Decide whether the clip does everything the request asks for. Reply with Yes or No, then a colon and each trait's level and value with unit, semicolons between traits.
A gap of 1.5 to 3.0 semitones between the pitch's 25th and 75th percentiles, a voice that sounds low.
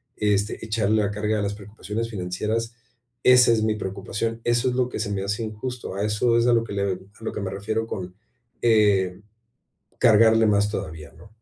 Yes: narrow, 2.4 semitones; low, 105 Hz